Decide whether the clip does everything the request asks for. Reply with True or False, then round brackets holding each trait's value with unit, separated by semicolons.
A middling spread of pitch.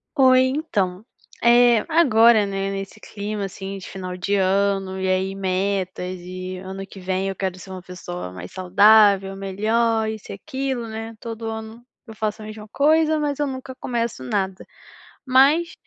True (3.7 semitones)